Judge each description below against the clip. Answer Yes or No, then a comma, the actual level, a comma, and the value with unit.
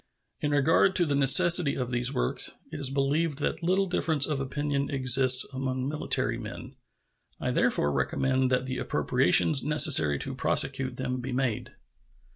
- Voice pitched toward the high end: No, low, 135 Hz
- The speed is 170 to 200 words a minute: No, average, 155 wpm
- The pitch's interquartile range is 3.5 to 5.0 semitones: No, narrow, 2.5 semitones